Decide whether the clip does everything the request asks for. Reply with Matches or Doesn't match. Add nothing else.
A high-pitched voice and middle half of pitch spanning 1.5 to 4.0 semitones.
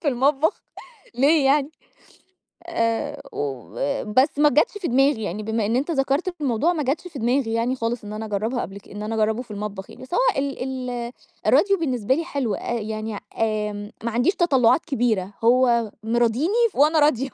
Doesn't match